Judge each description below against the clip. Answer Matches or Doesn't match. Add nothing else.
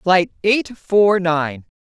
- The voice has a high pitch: Doesn't match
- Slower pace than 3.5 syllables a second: Matches